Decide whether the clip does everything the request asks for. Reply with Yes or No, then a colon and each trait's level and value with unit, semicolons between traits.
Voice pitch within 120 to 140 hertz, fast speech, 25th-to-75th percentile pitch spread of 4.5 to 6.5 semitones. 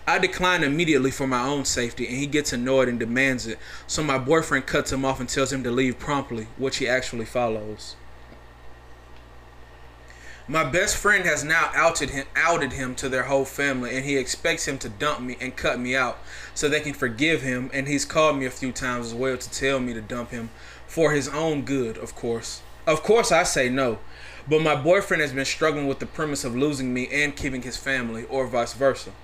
No: low, 135 Hz; fast, 215 wpm; average, 3.3 semitones